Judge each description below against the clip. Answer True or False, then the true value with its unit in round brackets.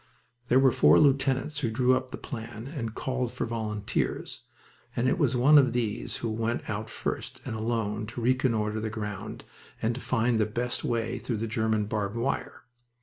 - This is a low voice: True (115 Hz)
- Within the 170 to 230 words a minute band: True (185 wpm)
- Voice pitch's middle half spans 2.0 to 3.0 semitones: True (2.7 semitones)